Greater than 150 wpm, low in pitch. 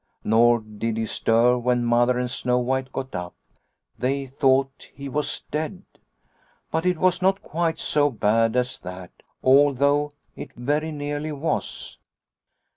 No: average, 145 wpm; low, 130 Hz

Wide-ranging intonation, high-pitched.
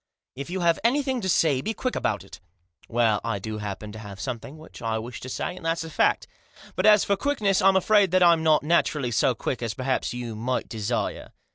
No: wide, 8.4 semitones; low, 135 Hz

